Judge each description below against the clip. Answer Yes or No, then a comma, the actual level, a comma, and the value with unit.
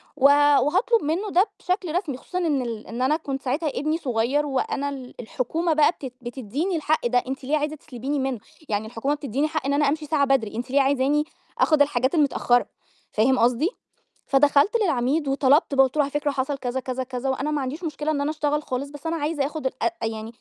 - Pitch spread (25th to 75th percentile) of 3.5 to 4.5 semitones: No, average, 3.0 semitones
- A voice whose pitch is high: Yes, very high, 280 Hz